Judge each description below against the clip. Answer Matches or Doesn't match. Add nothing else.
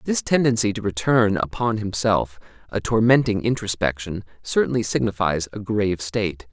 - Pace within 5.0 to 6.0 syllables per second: Matches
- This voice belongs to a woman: Doesn't match